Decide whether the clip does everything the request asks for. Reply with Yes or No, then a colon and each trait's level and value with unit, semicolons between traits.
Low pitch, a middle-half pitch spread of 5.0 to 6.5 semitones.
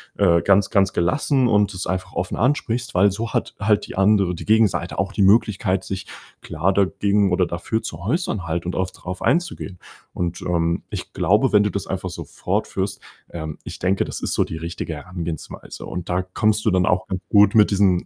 No: very low, 95 Hz; average, 2.8 semitones